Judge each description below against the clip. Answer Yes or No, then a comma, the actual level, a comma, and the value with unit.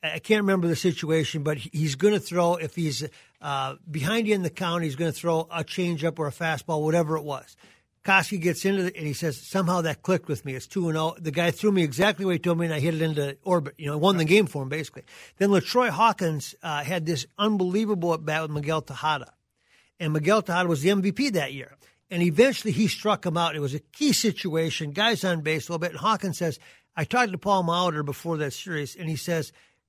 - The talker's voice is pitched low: No, medium, 170 Hz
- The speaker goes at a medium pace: No, fast, 245 wpm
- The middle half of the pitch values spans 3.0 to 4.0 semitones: Yes, average, 3.6 semitones